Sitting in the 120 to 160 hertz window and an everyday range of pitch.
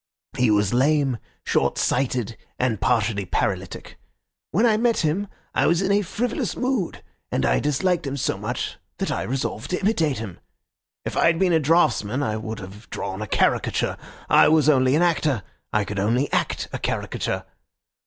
No: low, 135 Hz; wide, 7.6 semitones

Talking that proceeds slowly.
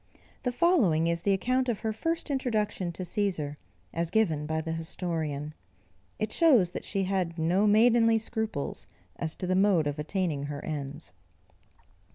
No: average, 160 wpm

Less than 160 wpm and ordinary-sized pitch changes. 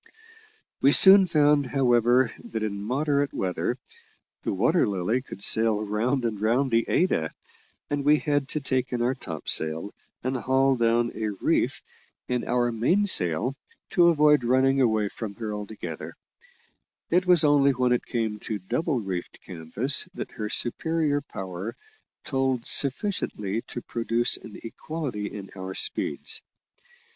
Yes: average, 140 wpm; average, 4.9 semitones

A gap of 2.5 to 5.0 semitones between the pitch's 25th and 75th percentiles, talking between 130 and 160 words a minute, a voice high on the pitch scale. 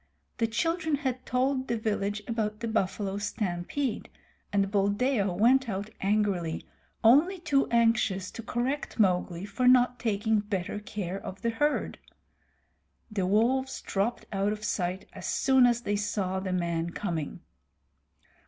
Yes: average, 4.1 semitones; average, 140 wpm; high, 215 Hz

